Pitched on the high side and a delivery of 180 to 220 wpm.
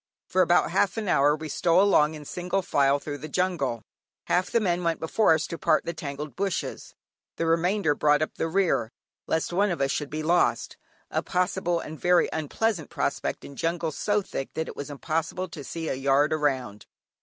No: medium, 160 Hz; average, 200 wpm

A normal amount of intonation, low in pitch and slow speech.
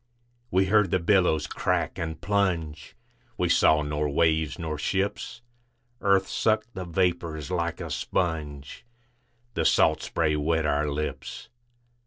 Yes: average, 3.7 semitones; very low, 85 Hz; slow, 130 wpm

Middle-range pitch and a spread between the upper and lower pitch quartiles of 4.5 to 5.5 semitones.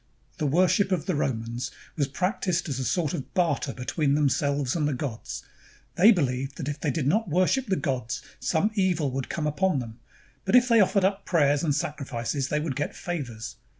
Yes: medium, 150 Hz; average, 5.2 semitones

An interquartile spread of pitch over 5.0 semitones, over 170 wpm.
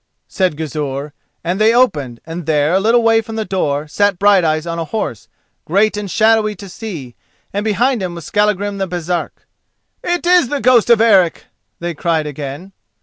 Yes: wide, 5.5 semitones; average, 180 wpm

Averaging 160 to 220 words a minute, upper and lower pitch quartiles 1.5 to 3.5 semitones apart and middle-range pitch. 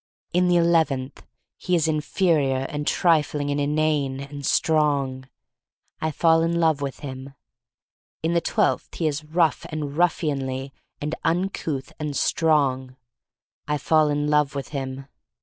No: average, 150 wpm; average, 2.7 semitones; medium, 150 Hz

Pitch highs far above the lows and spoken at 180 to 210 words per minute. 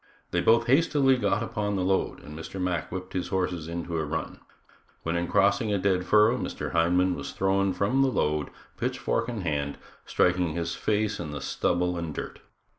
No: average, 3.6 semitones; average, 190 wpm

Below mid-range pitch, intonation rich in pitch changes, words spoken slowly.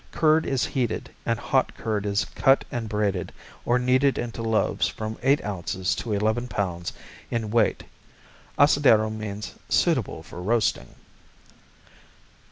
No: low, 110 Hz; average, 3.2 semitones; slow, 130 wpm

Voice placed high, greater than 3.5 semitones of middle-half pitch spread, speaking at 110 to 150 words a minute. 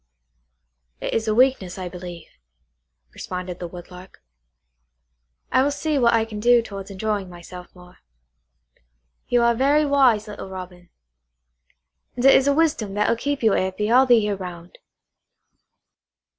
Yes: high, 210 Hz; average, 5.2 semitones; average, 145 wpm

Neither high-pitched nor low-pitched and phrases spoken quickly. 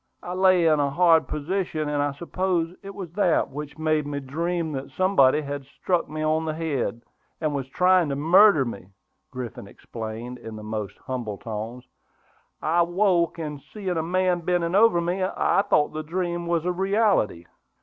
No: medium, 160 Hz; average, 180 wpm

